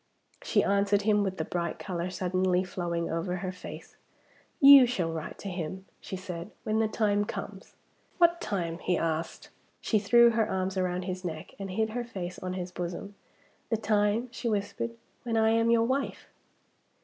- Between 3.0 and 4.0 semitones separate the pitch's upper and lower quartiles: Yes, average, 3.7 semitones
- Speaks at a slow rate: No, average, 175 wpm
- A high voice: Yes, high, 195 Hz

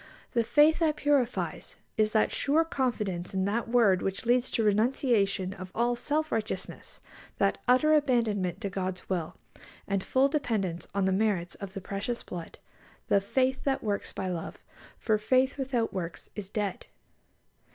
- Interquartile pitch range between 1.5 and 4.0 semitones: No, average, 5.0 semitones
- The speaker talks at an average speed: Yes, average, 160 wpm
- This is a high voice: Yes, high, 220 Hz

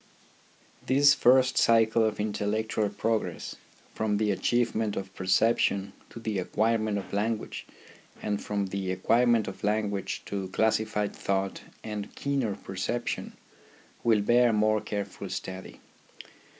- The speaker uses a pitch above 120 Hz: No, low, 105 Hz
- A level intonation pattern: Yes, narrow, 2.2 semitones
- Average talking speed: No, slow, 125 wpm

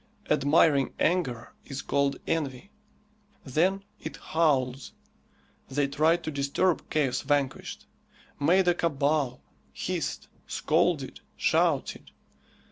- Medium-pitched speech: Yes, medium, 145 Hz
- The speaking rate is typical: No, slow, 95 wpm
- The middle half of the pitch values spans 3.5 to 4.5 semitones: No, average, 3.1 semitones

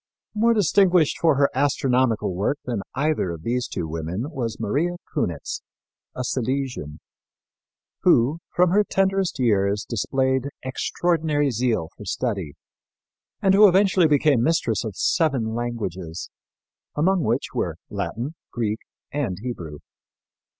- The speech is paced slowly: Yes, slow, 120 wpm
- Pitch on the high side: No, low, 130 Hz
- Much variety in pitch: Yes, wide, 6.5 semitones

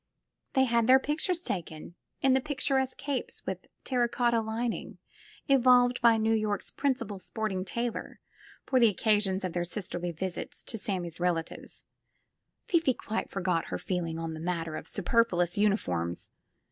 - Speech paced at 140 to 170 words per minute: Yes, average, 155 wpm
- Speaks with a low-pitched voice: No, high, 220 Hz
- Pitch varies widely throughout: Yes, wide, 5.8 semitones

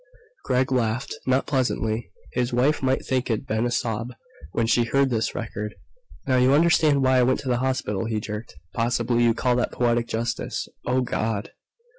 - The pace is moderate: Yes, average, 180 wpm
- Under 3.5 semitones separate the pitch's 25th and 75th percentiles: Yes, narrow, 2.4 semitones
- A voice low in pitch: Yes, low, 120 Hz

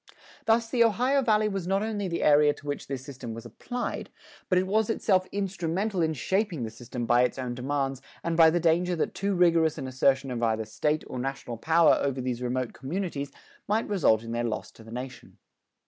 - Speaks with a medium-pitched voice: Yes, medium, 150 Hz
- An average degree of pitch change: No, wide, 7.3 semitones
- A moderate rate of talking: No, fast, 210 wpm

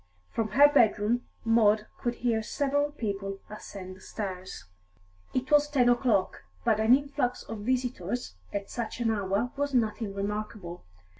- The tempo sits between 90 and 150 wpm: Yes, average, 145 wpm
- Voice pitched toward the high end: Yes, high, 225 Hz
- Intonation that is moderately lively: Yes, average, 3.6 semitones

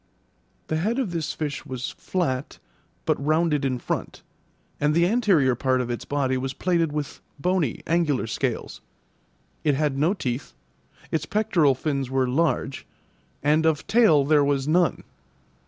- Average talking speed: Yes, average, 150 wpm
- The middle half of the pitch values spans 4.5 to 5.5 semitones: No, average, 3.9 semitones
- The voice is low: No, medium, 150 Hz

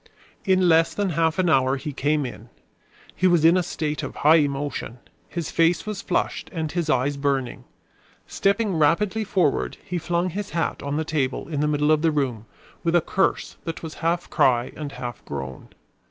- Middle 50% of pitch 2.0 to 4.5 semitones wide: Yes, average, 3.6 semitones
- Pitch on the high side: No, medium, 155 Hz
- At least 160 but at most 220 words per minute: Yes, average, 190 wpm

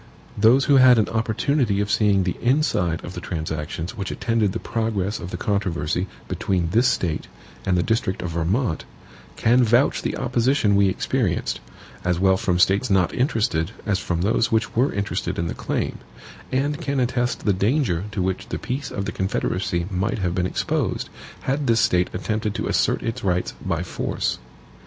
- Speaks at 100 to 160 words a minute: No, average, 180 wpm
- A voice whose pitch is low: Yes, low, 100 Hz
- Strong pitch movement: No, average, 4.8 semitones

